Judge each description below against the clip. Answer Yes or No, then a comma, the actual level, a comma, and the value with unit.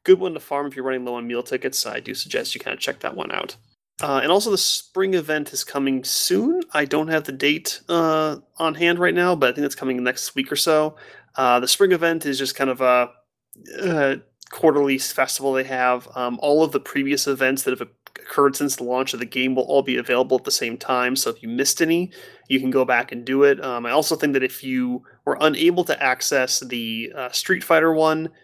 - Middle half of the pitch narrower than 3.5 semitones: No, average, 3.8 semitones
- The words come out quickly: Yes, fast, 240 wpm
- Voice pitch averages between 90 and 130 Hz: No, medium, 140 Hz